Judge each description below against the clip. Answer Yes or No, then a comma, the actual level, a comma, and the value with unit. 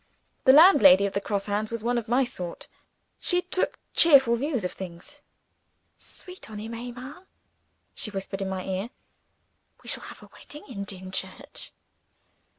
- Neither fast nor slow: Yes, average, 160 wpm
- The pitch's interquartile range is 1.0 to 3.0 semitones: No, wide, 5.5 semitones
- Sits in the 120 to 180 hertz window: No, high, 225 Hz